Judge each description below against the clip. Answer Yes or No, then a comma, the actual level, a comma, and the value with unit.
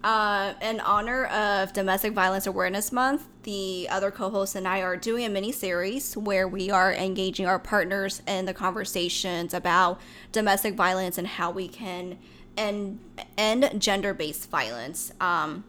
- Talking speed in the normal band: Yes, average, 155 wpm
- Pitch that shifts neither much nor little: No, narrow, 2.1 semitones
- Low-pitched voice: No, high, 195 Hz